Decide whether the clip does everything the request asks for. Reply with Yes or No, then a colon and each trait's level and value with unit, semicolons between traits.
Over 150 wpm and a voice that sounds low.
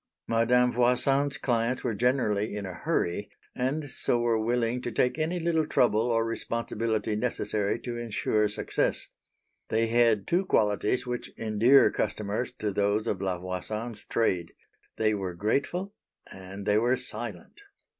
No: average, 145 wpm; low, 115 Hz